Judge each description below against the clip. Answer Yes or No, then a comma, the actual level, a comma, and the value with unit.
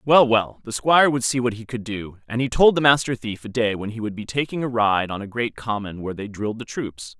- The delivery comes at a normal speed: No, fast, 285 wpm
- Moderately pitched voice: No, low, 115 Hz